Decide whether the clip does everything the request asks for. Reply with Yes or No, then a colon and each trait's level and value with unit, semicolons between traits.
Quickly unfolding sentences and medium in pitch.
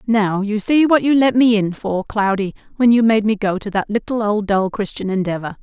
No: fast, 235 wpm; high, 215 Hz